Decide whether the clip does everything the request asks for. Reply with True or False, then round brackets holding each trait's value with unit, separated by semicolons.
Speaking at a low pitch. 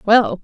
False (210 Hz)